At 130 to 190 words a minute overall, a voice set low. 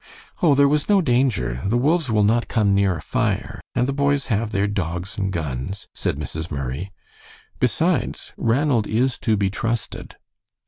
Yes: average, 170 wpm; low, 110 Hz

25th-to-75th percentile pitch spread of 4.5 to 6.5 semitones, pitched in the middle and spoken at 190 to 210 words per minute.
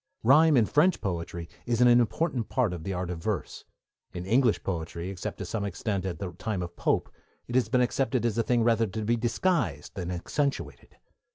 No: wide, 5.4 semitones; low, 110 Hz; average, 200 wpm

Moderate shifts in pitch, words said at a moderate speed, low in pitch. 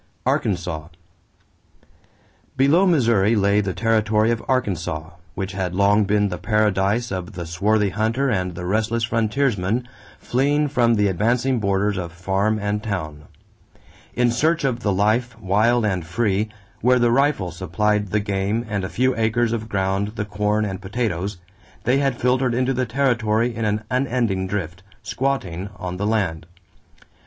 Yes: average, 3.7 semitones; average, 150 wpm; low, 105 Hz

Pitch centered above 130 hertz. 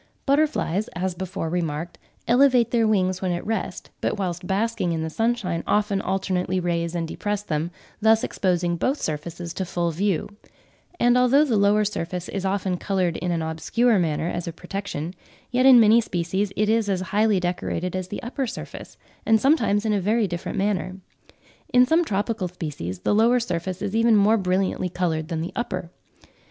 Yes: high, 190 Hz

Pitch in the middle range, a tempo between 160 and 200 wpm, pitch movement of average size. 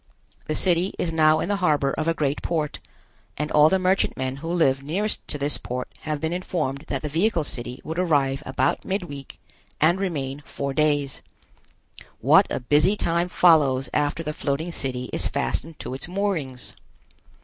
Yes: medium, 150 Hz; average, 170 wpm; average, 3.9 semitones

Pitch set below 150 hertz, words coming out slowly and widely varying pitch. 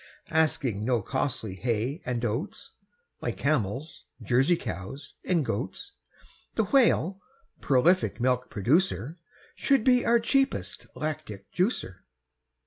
Yes: medium, 140 Hz; slow, 110 wpm; wide, 7.4 semitones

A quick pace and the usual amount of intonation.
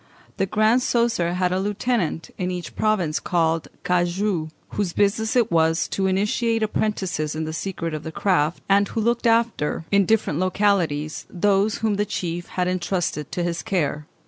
No: average, 170 wpm; average, 4.0 semitones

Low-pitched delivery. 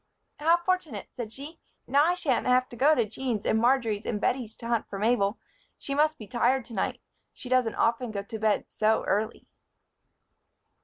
No: high, 240 Hz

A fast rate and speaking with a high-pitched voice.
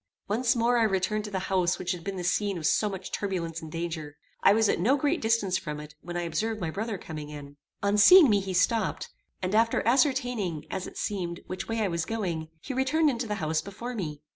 Yes: fast, 235 wpm; high, 195 Hz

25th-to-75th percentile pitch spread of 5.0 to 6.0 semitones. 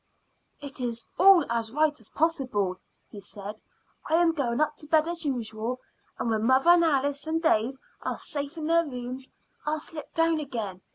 Yes: average, 5.3 semitones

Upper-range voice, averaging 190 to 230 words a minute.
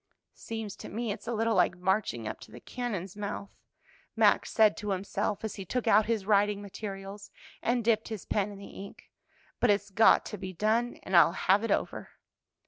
Yes: high, 205 Hz; average, 200 wpm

